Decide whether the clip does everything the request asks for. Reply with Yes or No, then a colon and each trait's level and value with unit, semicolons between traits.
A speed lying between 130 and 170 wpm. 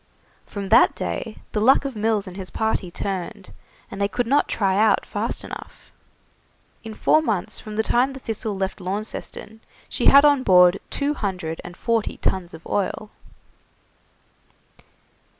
Yes: average, 155 wpm